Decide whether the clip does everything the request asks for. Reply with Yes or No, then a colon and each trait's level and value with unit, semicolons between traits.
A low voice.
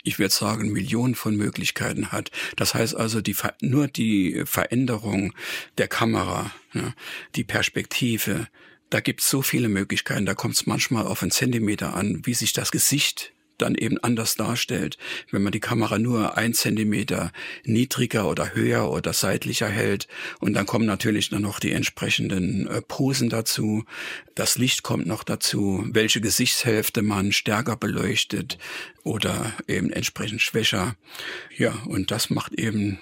Yes: low, 110 Hz